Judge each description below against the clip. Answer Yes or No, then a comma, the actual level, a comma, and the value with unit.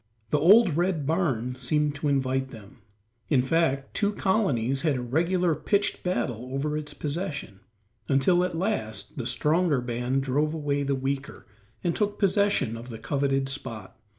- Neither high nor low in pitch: Yes, medium, 145 Hz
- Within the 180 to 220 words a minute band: No, average, 155 wpm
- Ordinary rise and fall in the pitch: Yes, average, 4.8 semitones